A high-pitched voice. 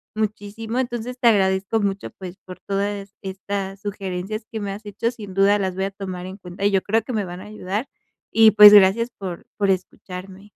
Yes: high, 200 Hz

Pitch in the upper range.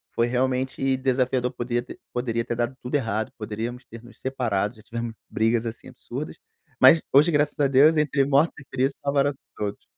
No: low, 125 Hz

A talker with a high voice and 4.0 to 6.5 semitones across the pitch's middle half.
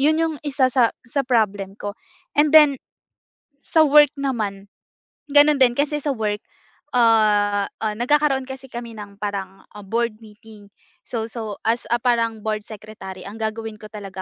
Yes: high, 225 Hz; average, 4.4 semitones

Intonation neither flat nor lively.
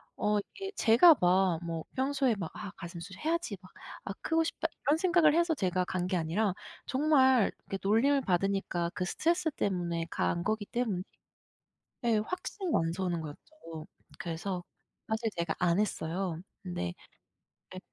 No: wide, 7.3 semitones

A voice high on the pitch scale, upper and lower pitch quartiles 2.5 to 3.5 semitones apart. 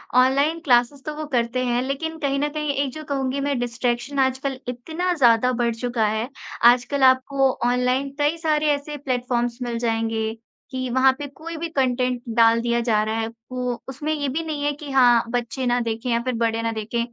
Yes: very high, 255 Hz; average, 3.1 semitones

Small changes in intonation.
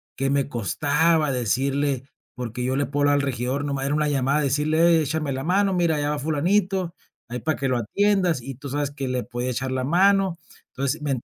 No: average, 3.3 semitones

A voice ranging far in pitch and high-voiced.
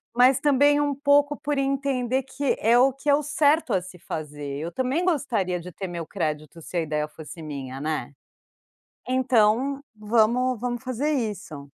Yes: wide, 8.3 semitones; high, 245 Hz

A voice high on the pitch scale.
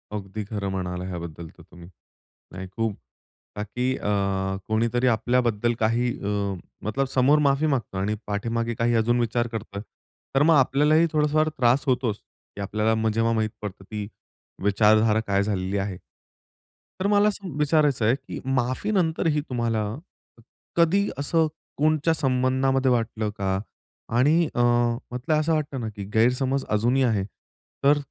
No: low, 120 Hz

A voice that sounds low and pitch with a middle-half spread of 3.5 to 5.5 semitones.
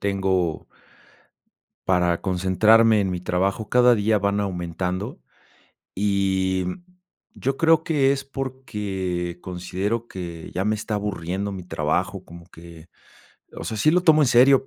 Yes: low, 100 Hz; average, 3.9 semitones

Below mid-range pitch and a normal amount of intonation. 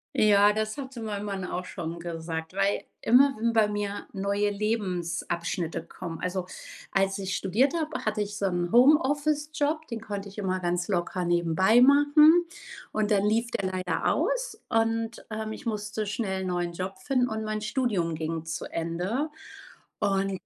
No: high, 205 Hz; average, 4.0 semitones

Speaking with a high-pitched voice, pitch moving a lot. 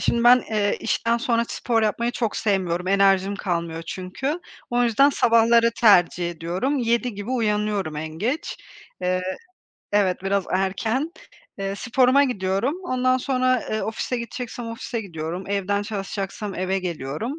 No: high, 210 Hz; average, 4.4 semitones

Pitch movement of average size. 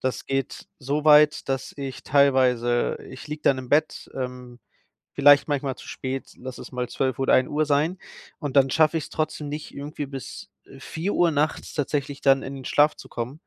No: narrow, 2.3 semitones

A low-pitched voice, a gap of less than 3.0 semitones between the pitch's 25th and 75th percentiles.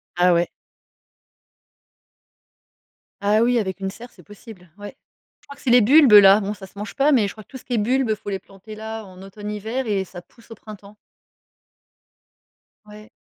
No: high, 210 Hz; narrow, 2.6 semitones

